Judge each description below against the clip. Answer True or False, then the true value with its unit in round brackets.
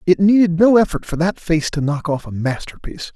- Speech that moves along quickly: True (230 wpm)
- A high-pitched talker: False (170 Hz)